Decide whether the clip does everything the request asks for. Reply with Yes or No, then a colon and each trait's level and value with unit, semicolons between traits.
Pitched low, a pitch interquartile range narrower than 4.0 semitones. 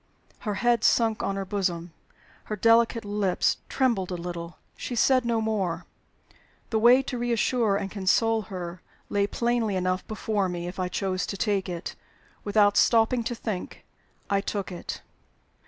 No: high, 205 Hz; average, 3.6 semitones